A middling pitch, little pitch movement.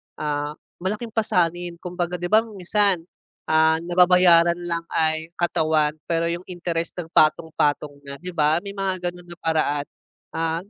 Yes: medium, 170 Hz; narrow, 2.1 semitones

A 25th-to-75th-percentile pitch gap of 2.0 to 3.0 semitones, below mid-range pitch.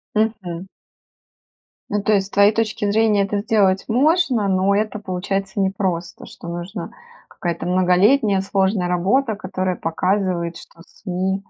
No: narrow, 2.5 semitones; high, 195 Hz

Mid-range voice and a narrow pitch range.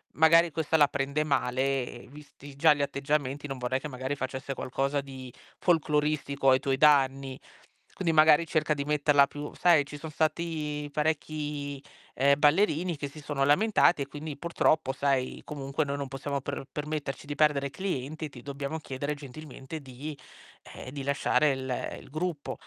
Yes: medium, 145 Hz; narrow, 1.9 semitones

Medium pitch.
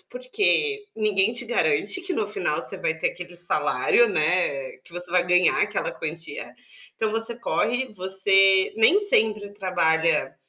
No: high, 195 Hz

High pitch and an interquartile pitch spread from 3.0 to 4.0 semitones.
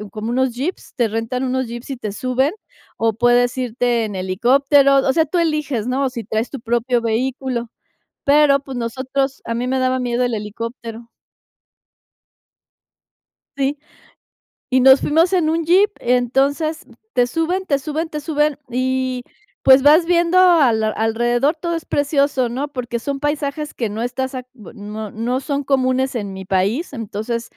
Yes: very high, 260 Hz; average, 3.4 semitones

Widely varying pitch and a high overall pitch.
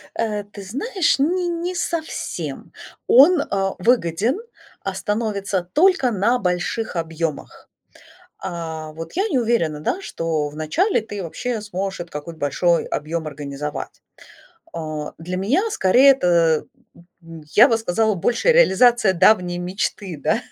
Yes: wide, 6.8 semitones; high, 195 Hz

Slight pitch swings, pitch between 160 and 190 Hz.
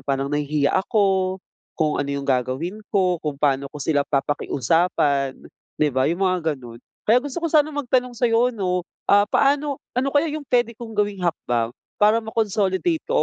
No: wide, 8.4 semitones; medium, 185 Hz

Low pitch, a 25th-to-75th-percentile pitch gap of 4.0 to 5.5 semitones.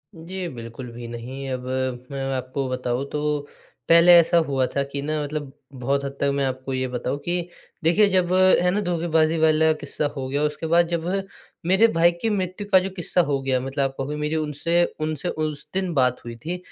No: medium, 150 Hz; average, 4.4 semitones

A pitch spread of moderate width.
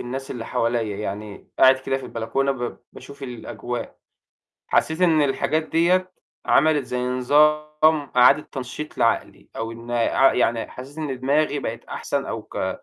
Yes: average, 4.0 semitones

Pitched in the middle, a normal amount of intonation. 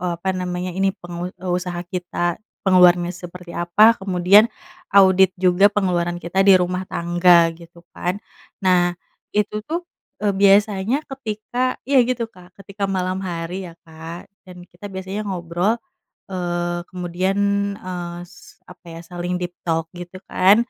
No: medium, 180 Hz; narrow, 1.8 semitones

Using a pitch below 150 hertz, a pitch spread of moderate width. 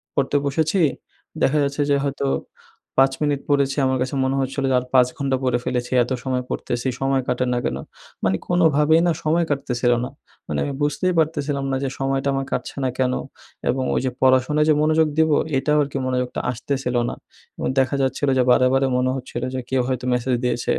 No: low, 135 Hz; narrow, 2.1 semitones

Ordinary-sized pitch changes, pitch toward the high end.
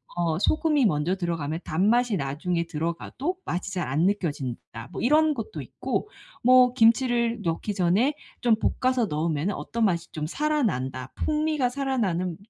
No: wide, 7.4 semitones; high, 195 Hz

